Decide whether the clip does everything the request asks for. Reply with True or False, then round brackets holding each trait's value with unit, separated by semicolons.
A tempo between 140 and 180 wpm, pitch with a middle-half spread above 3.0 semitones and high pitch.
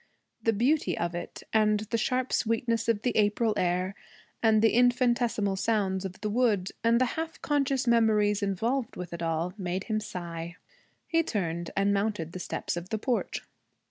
True (175 wpm; 4.3 semitones; 215 Hz)